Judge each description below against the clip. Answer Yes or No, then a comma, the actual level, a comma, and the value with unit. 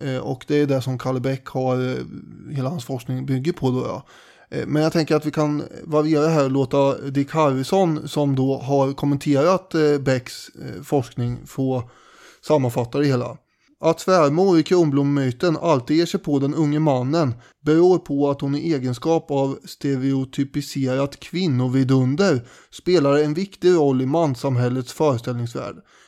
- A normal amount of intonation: Yes, average, 3.0 semitones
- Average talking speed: Yes, average, 150 wpm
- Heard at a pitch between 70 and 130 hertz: No, medium, 140 Hz